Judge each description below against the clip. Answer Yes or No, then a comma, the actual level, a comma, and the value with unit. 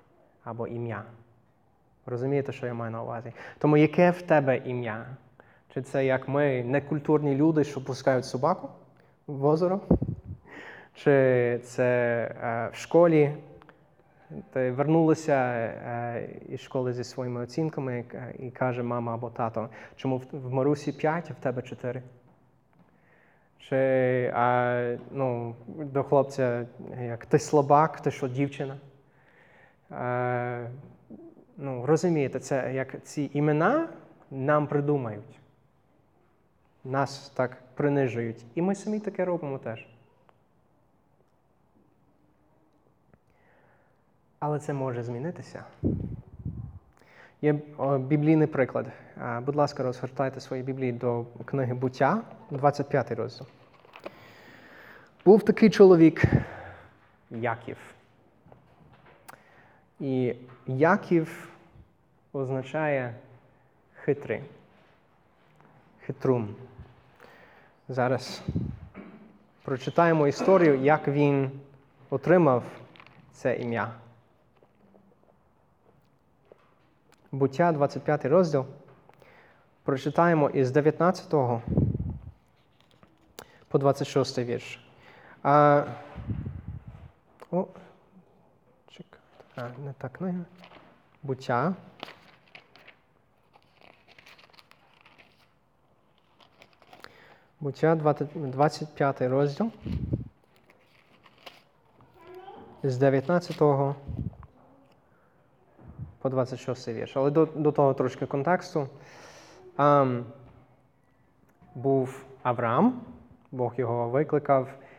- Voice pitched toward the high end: No, low, 135 Hz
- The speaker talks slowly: Yes, slow, 75 wpm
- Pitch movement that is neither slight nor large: Yes, average, 3.2 semitones